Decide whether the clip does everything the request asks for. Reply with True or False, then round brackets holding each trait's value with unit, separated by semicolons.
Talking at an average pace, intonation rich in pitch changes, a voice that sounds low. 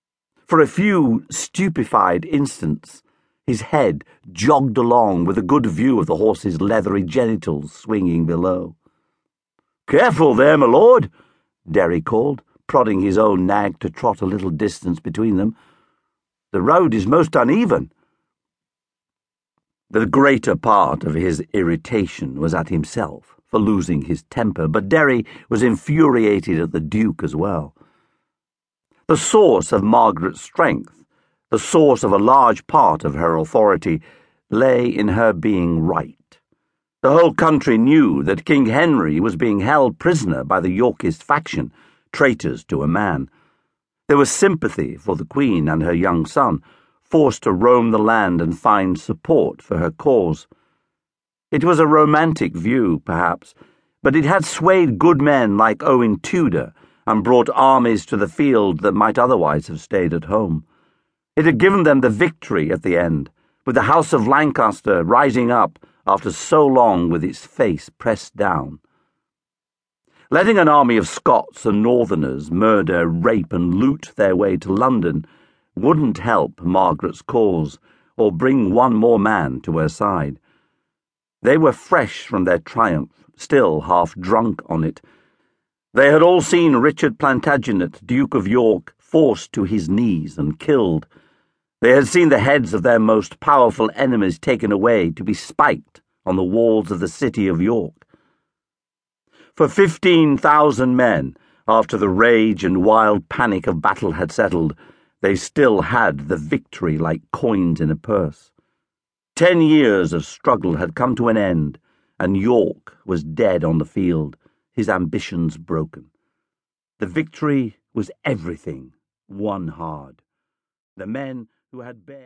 True (150 wpm; 8.7 semitones; 110 Hz)